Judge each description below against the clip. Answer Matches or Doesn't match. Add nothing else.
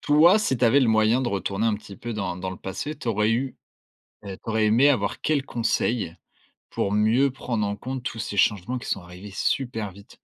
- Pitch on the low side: Matches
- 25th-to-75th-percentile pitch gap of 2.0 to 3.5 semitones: Doesn't match